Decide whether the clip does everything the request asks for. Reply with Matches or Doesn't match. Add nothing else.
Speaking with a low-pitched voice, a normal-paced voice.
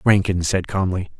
Matches